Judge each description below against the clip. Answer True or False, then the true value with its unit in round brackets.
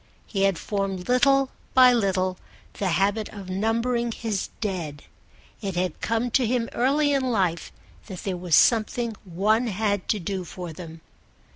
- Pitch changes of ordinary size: True (4.2 semitones)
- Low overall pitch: False (205 Hz)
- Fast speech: False (155 wpm)